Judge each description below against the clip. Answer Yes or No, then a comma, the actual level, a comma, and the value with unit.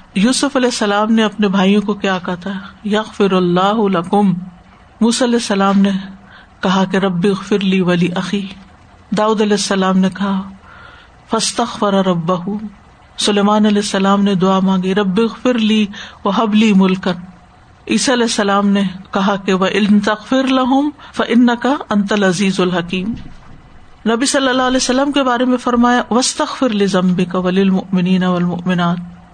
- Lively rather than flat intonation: No, average, 3.2 semitones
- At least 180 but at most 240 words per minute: No, average, 135 wpm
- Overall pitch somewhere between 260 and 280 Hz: No, high, 205 Hz